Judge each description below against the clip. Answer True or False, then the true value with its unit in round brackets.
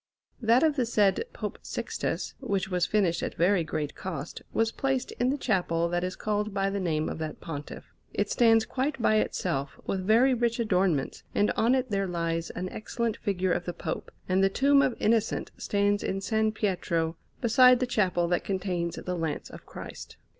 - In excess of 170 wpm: True (190 wpm)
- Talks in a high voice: True (195 Hz)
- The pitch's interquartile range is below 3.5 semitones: False (4.7 semitones)